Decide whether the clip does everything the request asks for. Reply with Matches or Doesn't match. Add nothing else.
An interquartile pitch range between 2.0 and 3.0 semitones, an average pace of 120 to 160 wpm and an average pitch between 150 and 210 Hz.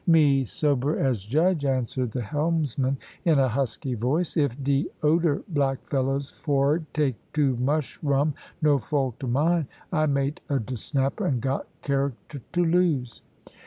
Doesn't match